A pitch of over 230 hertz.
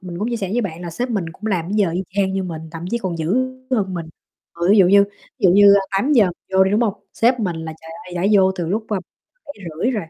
No: high, 190 Hz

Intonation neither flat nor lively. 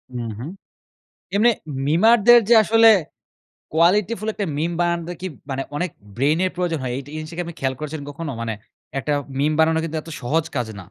Yes: average, 4.4 semitones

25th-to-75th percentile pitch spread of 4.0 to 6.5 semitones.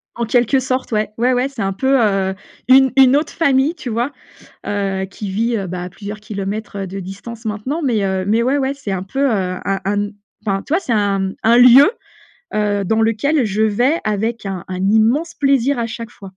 Yes: average, 4.7 semitones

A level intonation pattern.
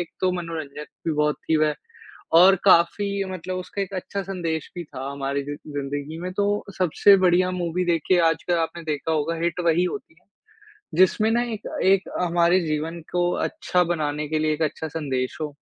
No: average, 3.2 semitones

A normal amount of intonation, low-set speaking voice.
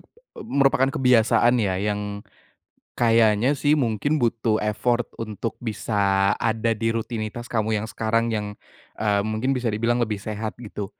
No: narrow, 2.2 semitones; low, 110 Hz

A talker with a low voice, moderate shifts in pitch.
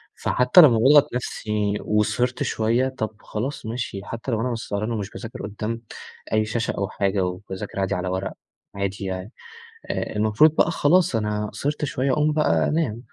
Yes: low, 110 Hz; average, 3.7 semitones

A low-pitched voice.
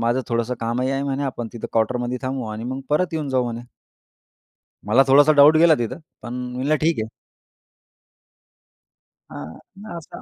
Yes: low, 130 Hz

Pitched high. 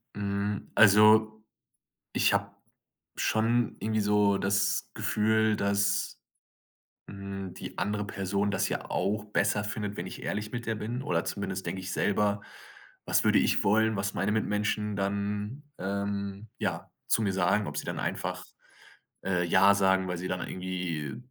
No: low, 100 Hz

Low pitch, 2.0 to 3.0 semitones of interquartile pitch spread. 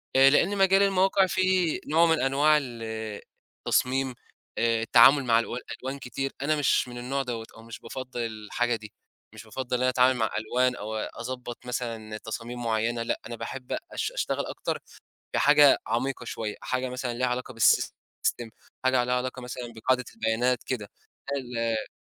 Yes: low, 125 Hz; narrow, 2.5 semitones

